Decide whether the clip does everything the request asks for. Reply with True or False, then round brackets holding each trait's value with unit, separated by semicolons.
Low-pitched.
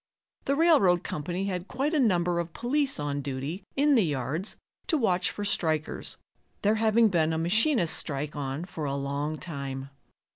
False (175 Hz)